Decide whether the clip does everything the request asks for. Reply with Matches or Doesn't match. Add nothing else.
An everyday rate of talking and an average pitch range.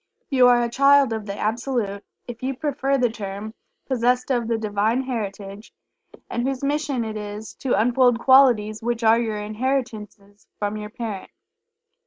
Matches